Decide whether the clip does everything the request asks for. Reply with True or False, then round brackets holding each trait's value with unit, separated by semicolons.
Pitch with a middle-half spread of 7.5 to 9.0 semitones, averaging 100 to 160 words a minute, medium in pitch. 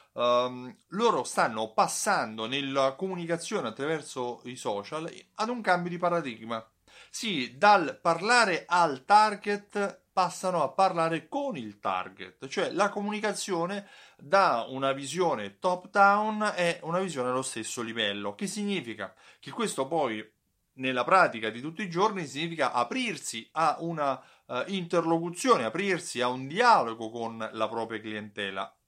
True (8.1 semitones; 135 wpm; 165 Hz)